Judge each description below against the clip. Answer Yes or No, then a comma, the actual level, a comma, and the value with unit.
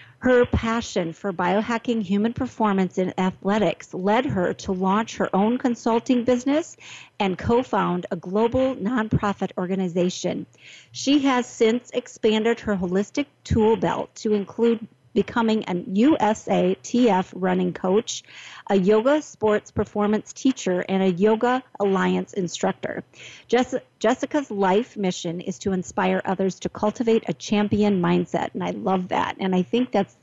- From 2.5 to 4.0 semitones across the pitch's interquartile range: Yes, average, 3.7 semitones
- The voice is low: No, high, 210 Hz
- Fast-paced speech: No, average, 140 wpm